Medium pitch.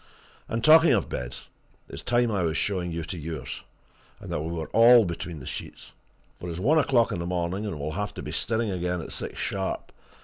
No: very low, 90 Hz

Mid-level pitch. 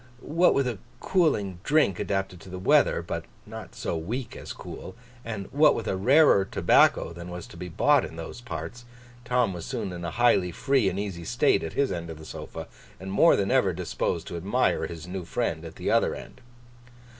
No: very low, 95 Hz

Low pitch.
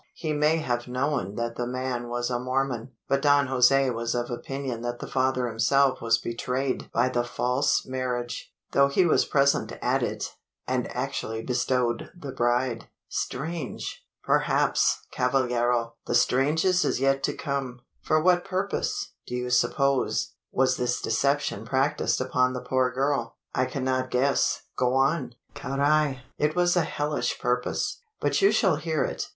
Yes: low, 130 Hz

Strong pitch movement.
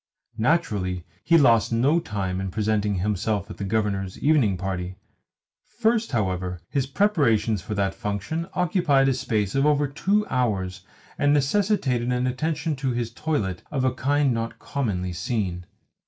Yes: wide, 6.7 semitones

